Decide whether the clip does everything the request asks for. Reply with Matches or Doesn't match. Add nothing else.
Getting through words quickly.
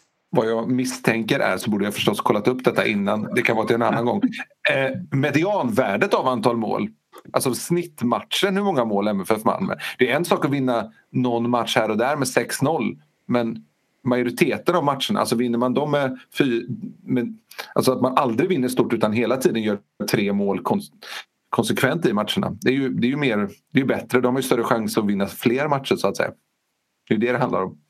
Matches